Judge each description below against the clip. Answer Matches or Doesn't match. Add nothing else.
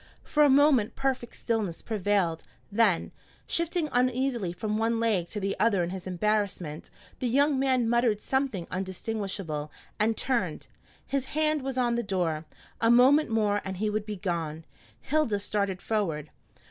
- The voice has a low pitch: Doesn't match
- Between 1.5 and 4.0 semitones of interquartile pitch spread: Doesn't match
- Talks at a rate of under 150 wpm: Doesn't match